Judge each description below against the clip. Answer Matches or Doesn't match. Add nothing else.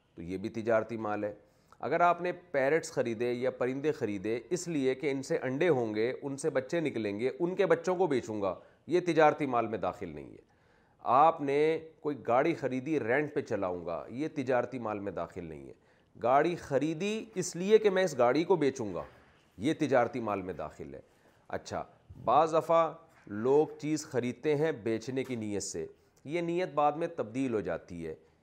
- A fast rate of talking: Matches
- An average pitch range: Doesn't match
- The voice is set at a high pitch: Doesn't match